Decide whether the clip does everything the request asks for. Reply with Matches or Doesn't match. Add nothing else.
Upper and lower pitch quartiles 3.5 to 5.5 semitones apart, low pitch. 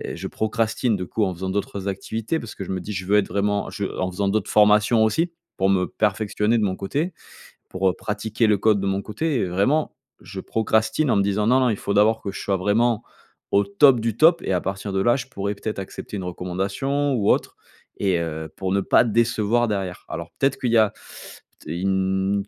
Doesn't match